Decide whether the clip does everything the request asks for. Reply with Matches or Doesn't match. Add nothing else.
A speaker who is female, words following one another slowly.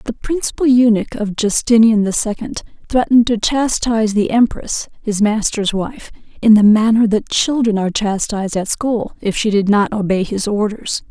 Doesn't match